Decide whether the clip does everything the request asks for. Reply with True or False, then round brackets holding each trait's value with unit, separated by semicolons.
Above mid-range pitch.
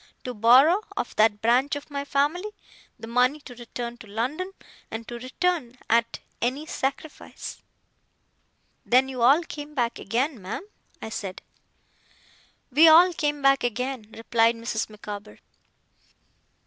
True (250 Hz)